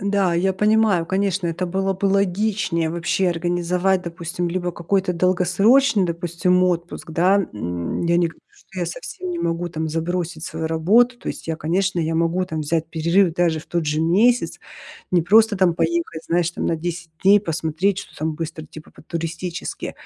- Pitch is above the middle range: No, medium, 175 Hz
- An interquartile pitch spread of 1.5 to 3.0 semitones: Yes, average, 2.7 semitones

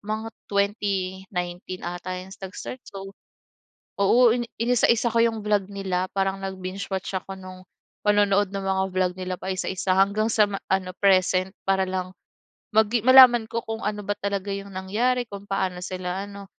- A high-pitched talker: Yes, high, 195 Hz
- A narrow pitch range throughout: Yes, narrow, 2.0 semitones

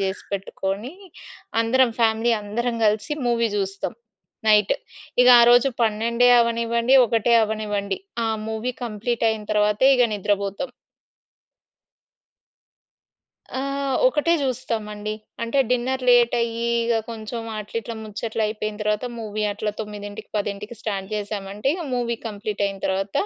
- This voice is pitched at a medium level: No, high, 220 Hz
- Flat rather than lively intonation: Yes, narrow, 2.3 semitones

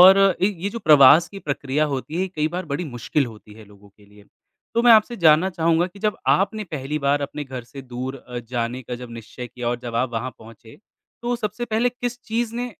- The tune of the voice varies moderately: No, wide, 8.4 semitones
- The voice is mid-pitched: Yes, medium, 145 Hz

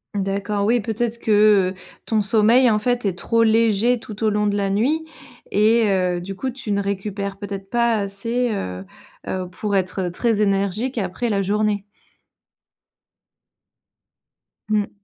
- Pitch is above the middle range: Yes, high, 210 Hz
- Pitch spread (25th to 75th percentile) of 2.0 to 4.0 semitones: Yes, average, 2.7 semitones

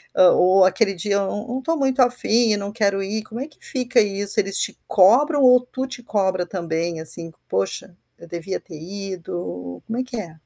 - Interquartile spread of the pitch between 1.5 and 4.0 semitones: No, average, 5.3 semitones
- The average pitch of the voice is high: Yes, high, 200 Hz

